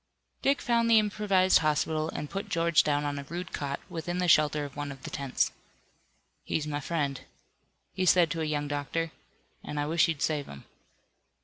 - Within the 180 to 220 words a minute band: Yes, average, 190 wpm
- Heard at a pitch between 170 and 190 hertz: No, medium, 155 Hz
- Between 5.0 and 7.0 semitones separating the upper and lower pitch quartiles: No, average, 3.2 semitones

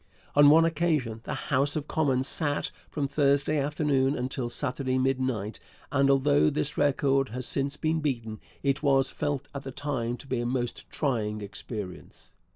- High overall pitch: No, low, 135 Hz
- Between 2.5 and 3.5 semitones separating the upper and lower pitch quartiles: Yes, average, 2.8 semitones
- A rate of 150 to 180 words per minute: Yes, average, 160 wpm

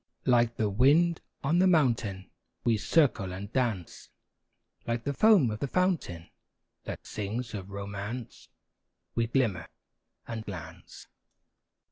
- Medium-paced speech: No, slow, 120 wpm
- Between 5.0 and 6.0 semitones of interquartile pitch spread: Yes, wide, 5.4 semitones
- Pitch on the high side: No, low, 115 Hz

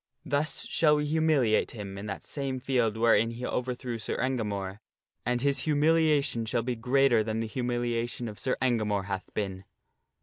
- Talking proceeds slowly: No, average, 165 wpm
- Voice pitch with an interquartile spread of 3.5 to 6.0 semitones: Yes, average, 3.9 semitones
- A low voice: Yes, low, 120 Hz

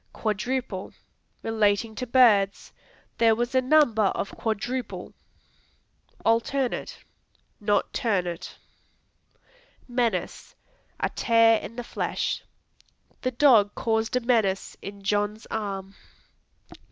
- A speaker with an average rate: No, slow, 95 wpm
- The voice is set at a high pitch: Yes, high, 225 Hz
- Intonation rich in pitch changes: No, average, 3.0 semitones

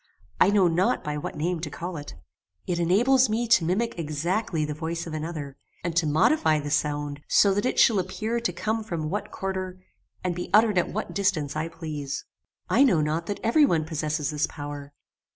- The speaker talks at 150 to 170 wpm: No, fast, 205 wpm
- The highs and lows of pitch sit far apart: No, average, 4.6 semitones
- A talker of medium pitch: Yes, medium, 170 Hz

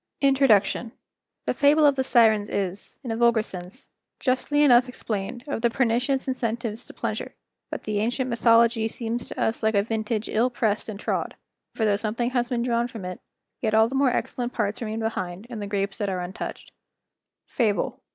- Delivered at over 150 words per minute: Yes, average, 185 wpm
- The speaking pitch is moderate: No, high, 230 Hz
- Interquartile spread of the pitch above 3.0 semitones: No, average, 2.7 semitones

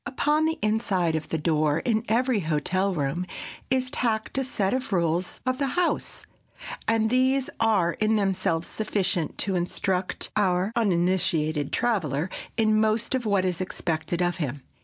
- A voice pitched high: Yes, high, 195 Hz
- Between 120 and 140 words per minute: No, average, 155 wpm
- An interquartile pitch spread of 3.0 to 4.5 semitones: No, average, 5.0 semitones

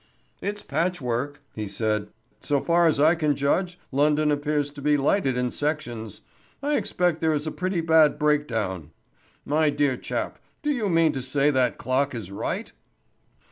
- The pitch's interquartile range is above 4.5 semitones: No, average, 3.7 semitones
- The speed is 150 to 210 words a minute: Yes, average, 165 wpm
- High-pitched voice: No, medium, 145 Hz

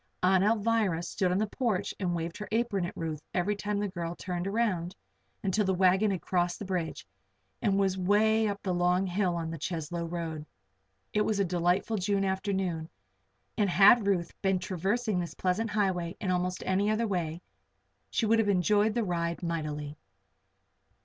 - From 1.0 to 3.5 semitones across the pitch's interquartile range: Yes, average, 3.0 semitones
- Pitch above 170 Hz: Yes, high, 190 Hz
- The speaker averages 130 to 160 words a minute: No, average, 175 wpm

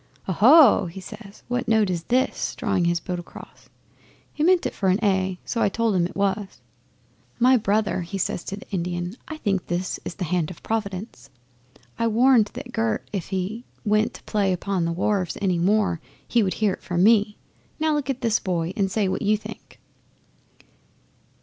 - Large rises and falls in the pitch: No, average, 3.5 semitones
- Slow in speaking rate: No, average, 185 wpm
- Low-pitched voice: No, high, 200 Hz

